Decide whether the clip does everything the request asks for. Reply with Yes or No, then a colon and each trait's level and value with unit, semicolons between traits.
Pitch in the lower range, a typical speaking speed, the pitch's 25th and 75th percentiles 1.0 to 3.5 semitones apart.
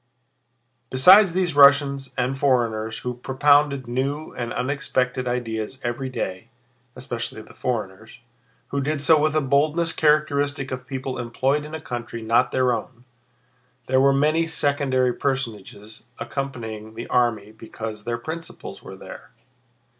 No: low, 130 Hz; slow, 130 wpm; average, 3.1 semitones